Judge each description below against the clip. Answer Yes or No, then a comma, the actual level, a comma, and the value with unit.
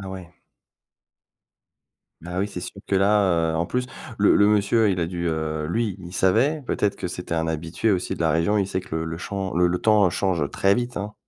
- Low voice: Yes, very low, 95 Hz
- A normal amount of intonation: Yes, average, 3.4 semitones